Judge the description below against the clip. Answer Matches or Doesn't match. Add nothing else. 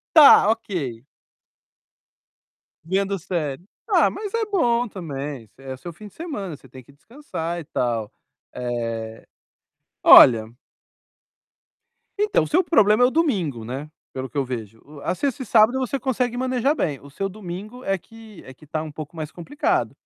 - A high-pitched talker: Doesn't match